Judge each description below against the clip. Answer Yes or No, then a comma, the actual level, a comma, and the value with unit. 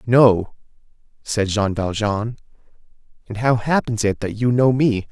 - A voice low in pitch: Yes, low, 115 Hz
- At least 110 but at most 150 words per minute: Yes, average, 140 wpm